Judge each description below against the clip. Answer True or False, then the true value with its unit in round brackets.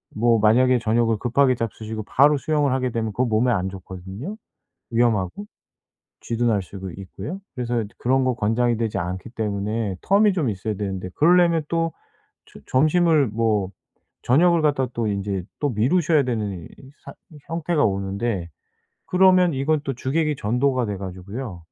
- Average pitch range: False (5.8 semitones)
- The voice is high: False (120 Hz)